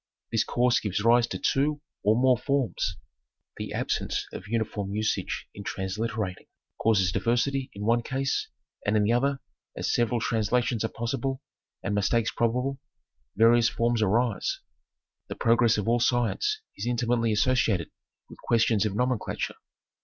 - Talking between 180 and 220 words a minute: No, average, 145 wpm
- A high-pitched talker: No, low, 115 Hz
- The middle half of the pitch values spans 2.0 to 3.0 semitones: Yes, narrow, 2.5 semitones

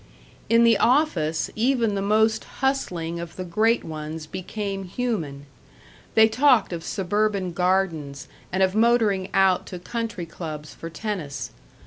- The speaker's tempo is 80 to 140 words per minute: Yes, slow, 135 wpm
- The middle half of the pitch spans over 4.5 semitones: Yes, average, 4.9 semitones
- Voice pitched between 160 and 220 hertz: Yes, high, 190 Hz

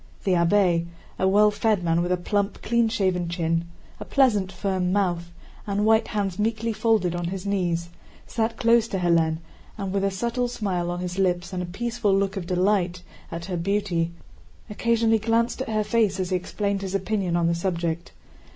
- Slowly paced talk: No, average, 190 wpm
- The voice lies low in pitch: No, high, 195 Hz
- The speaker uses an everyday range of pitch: Yes, average, 3.3 semitones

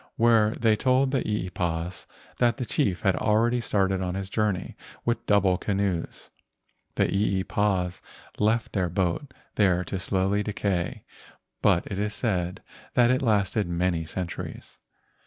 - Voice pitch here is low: Yes, low, 100 Hz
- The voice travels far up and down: No, average, 3.2 semitones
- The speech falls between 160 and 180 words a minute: No, average, 140 wpm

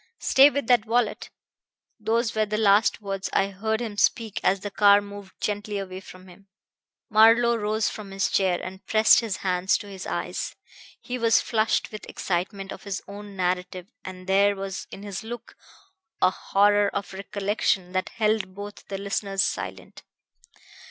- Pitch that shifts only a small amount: Yes, narrow, 2.1 semitones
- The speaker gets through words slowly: No, average, 170 wpm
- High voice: Yes, high, 200 Hz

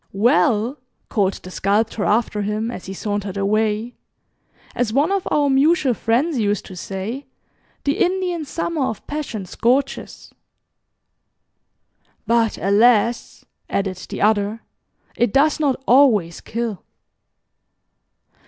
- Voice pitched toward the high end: Yes, high, 230 Hz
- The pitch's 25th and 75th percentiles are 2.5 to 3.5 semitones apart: No, average, 5.2 semitones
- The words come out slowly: Yes, slow, 115 wpm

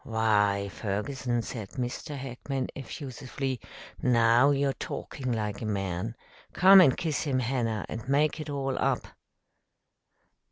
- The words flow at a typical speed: No, slow, 125 wpm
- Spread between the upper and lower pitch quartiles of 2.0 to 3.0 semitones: No, average, 3.7 semitones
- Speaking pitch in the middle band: No, low, 125 Hz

